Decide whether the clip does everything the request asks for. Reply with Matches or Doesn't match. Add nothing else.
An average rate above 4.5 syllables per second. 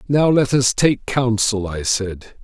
Doesn't match